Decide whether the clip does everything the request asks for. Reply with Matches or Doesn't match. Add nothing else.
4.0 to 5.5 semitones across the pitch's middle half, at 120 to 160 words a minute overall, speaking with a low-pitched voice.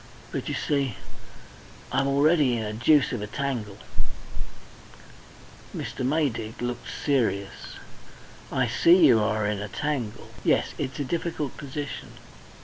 Matches